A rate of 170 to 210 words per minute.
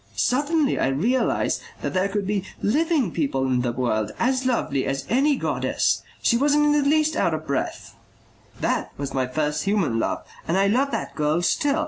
Yes: average, 185 wpm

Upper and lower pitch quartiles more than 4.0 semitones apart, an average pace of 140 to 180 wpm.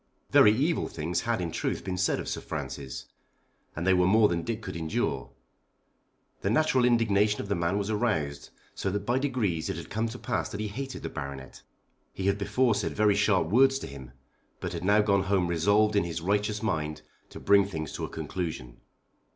No: average, 4.4 semitones; fast, 205 wpm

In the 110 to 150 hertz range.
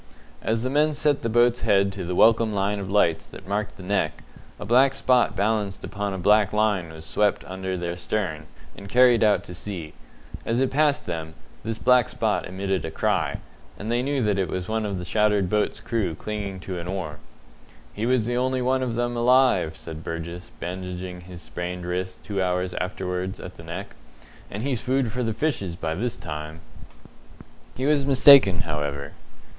No: low, 100 Hz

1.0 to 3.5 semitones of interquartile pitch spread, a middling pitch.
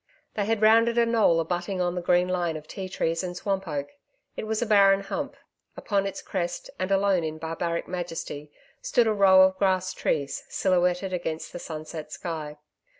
Yes: average, 3.1 semitones; medium, 180 Hz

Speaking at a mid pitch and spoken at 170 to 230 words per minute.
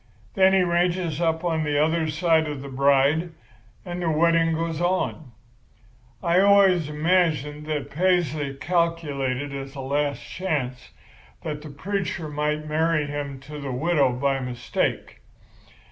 No: medium, 155 Hz; average, 140 wpm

